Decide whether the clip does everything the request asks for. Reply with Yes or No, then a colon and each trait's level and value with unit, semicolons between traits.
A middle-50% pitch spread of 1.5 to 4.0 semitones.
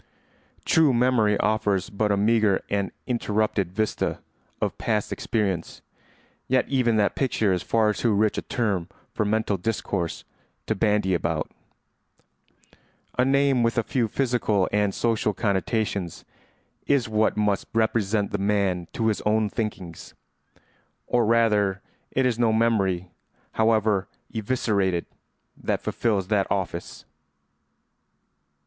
Yes: narrow, 2.6 semitones